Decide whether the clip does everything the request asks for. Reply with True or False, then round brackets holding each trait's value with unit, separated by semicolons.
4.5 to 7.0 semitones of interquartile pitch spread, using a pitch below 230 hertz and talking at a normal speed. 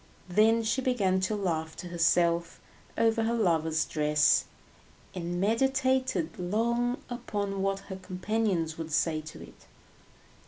False (5.2 semitones; 190 Hz; 125 wpm)